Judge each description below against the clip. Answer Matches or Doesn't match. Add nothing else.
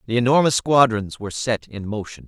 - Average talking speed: Matches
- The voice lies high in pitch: Doesn't match